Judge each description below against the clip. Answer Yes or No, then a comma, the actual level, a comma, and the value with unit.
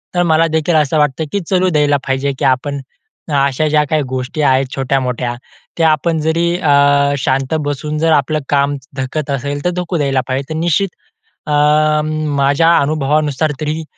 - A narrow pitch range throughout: Yes, narrow, 2.2 semitones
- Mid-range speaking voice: Yes, medium, 150 Hz